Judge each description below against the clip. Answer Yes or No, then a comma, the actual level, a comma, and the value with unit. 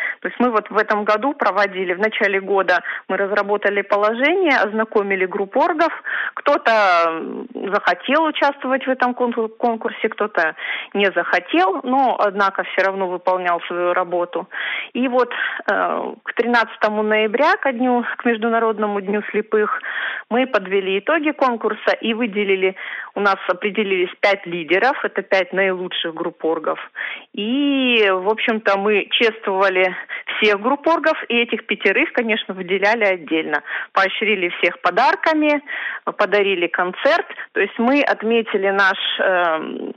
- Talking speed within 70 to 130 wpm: Yes, average, 125 wpm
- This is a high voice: Yes, high, 210 Hz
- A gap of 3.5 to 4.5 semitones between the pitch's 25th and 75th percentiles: Yes, average, 3.8 semitones